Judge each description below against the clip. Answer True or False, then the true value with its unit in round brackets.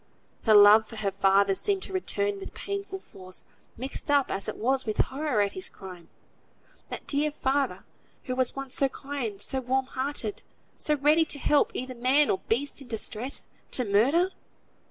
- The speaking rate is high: False (175 wpm)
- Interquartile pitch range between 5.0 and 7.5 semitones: True (5.4 semitones)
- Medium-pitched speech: False (260 Hz)